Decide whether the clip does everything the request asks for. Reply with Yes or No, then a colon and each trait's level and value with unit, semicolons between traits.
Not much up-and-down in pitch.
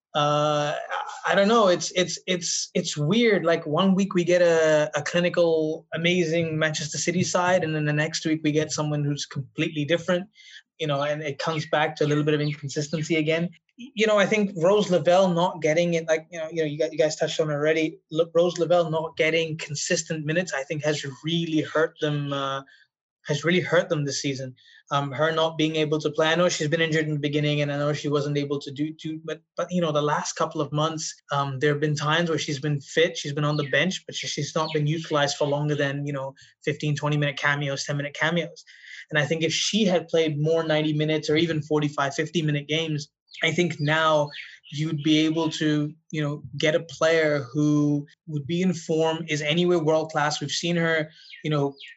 Yes: narrow, 2.0 semitones